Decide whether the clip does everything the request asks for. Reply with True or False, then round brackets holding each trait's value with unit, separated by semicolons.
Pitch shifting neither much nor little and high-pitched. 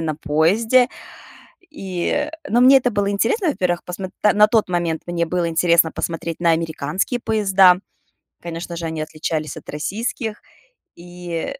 False (4.3 semitones; 175 Hz)